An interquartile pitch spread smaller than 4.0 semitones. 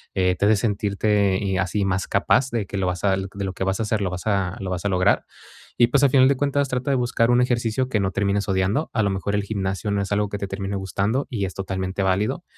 Yes: average, 2.9 semitones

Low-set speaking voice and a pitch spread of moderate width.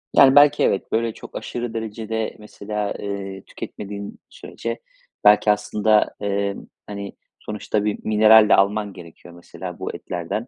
No: low, 105 Hz; narrow, 1.7 semitones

